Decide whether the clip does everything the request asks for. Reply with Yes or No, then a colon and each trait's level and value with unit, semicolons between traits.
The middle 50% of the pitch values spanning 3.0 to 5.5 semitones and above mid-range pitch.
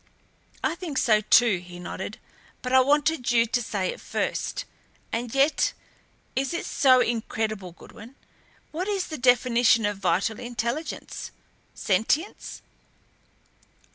Yes: average, 4.3 semitones; high, 240 Hz